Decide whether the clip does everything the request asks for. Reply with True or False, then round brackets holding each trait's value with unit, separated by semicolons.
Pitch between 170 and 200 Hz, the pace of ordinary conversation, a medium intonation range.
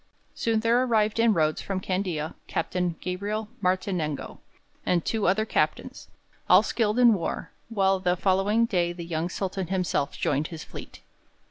True (190 Hz; 150 wpm; 3.8 semitones)